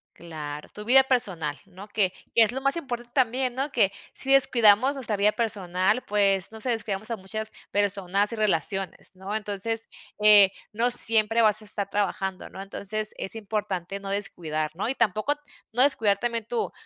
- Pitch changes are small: No, average, 3.1 semitones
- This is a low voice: No, high, 210 Hz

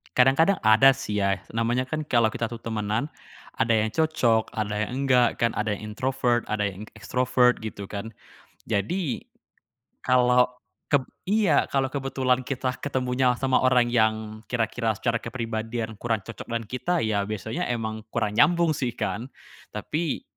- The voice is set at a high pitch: No, low, 120 Hz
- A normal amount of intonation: Yes, average, 3.0 semitones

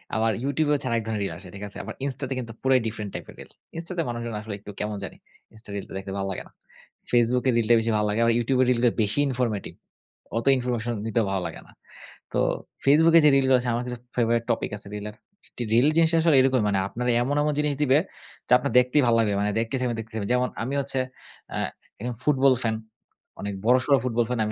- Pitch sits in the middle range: No, low, 120 Hz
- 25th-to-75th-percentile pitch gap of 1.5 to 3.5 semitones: Yes, average, 3.2 semitones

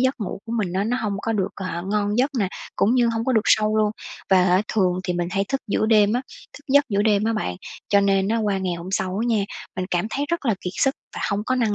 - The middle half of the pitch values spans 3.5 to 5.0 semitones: No, average, 3.1 semitones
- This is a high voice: Yes, high, 210 Hz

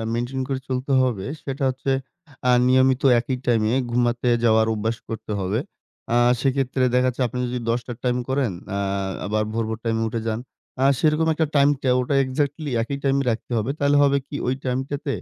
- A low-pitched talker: Yes, low, 130 Hz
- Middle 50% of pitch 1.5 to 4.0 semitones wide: Yes, average, 2.9 semitones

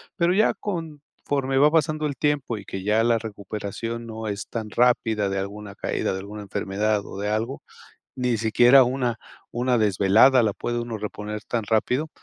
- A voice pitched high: No, low, 115 Hz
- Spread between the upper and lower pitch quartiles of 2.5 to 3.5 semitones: No, average, 3.9 semitones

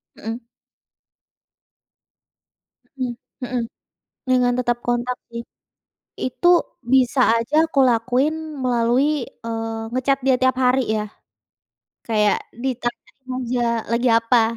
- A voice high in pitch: Yes, high, 245 Hz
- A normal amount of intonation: No, narrow, 1.8 semitones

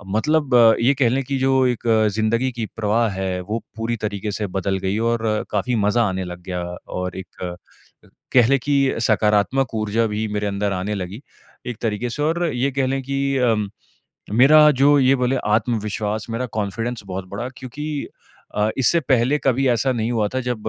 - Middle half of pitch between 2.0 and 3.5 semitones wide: No, average, 4.0 semitones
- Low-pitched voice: Yes, low, 115 Hz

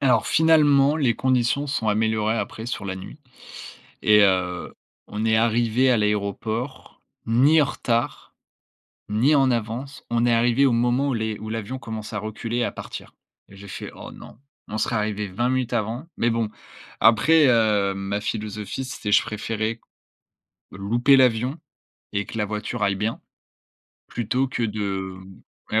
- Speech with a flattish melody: No, average, 3.0 semitones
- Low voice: Yes, low, 115 Hz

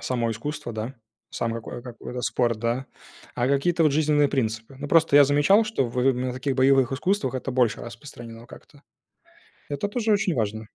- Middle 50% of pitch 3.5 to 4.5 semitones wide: Yes, average, 3.8 semitones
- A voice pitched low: Yes, low, 130 Hz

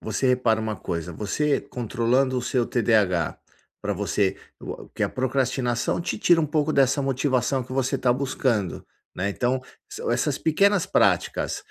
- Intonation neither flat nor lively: Yes, average, 3.8 semitones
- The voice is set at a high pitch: No, low, 125 Hz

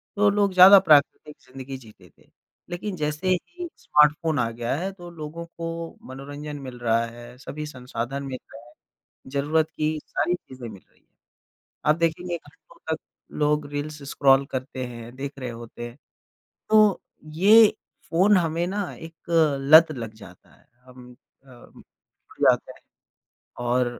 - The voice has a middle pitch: Yes, medium, 150 Hz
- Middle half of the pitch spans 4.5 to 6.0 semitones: Yes, average, 4.9 semitones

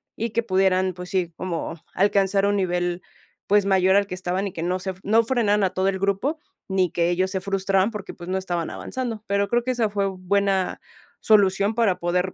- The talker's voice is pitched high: Yes, high, 195 Hz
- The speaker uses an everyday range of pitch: No, narrow, 1.7 semitones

